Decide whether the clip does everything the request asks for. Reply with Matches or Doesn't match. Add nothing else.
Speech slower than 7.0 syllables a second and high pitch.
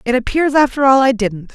Matches